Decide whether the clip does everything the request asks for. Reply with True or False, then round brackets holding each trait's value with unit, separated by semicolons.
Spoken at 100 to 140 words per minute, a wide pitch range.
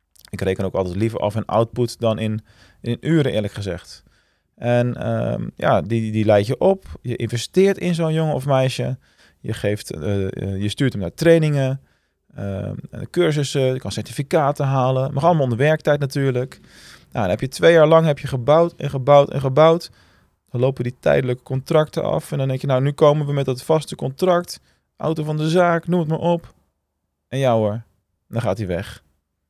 False (200 wpm; 6.5 semitones)